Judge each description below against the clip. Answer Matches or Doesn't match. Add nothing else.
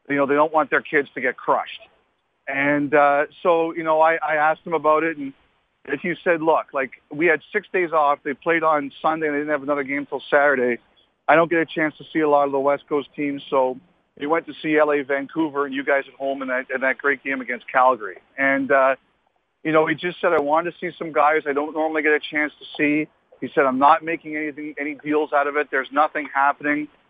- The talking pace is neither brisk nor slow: Doesn't match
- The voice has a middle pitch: Matches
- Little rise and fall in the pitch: Matches